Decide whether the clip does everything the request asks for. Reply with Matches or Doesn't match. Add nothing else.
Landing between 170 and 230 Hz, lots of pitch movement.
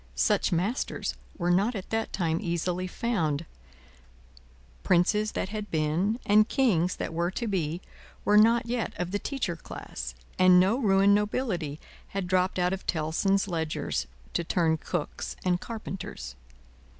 Doesn't match